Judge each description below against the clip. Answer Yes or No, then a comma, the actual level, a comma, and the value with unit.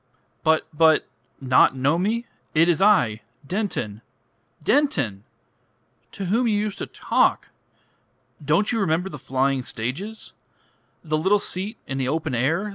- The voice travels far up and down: Yes, wide, 7.4 semitones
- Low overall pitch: No, medium, 160 Hz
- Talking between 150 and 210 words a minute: No, slow, 135 wpm